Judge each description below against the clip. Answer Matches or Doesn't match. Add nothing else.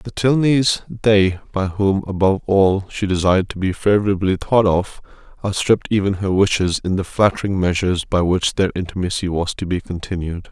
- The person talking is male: Matches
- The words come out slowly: Doesn't match